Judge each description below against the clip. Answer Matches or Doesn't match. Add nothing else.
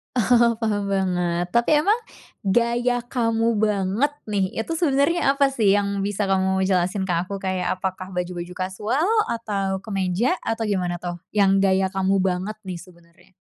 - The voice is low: Doesn't match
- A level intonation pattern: Doesn't match